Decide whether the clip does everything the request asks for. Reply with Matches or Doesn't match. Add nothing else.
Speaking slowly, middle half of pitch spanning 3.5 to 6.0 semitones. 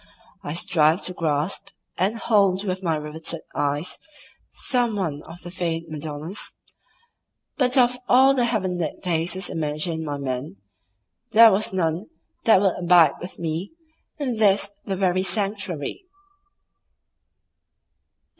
Matches